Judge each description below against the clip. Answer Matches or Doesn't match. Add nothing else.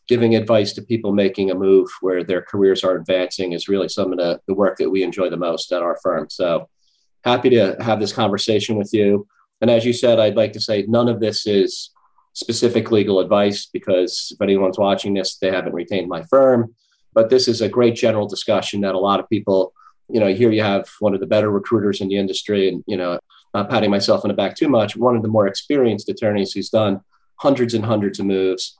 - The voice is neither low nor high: Doesn't match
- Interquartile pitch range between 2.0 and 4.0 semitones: Matches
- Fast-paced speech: Matches